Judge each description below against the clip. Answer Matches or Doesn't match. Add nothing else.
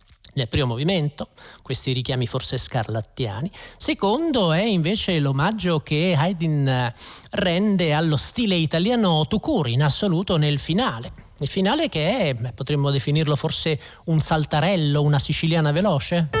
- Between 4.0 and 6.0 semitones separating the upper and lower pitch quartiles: Matches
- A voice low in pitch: Doesn't match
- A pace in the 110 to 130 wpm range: Matches